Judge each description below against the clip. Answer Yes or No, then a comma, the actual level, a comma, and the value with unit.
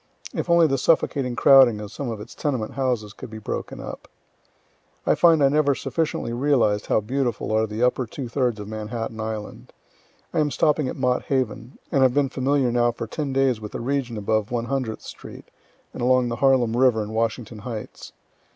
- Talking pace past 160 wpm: Yes, average, 195 wpm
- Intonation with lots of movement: No, average, 3.6 semitones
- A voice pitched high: No, low, 125 Hz